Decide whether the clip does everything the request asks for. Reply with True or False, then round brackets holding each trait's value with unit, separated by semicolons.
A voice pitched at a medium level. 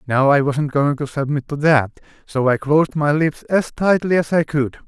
True (145 Hz)